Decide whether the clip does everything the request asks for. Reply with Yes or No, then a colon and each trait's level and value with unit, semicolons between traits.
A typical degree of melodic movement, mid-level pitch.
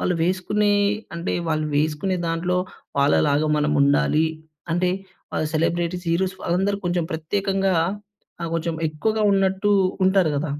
Yes: average, 3.4 semitones; medium, 175 Hz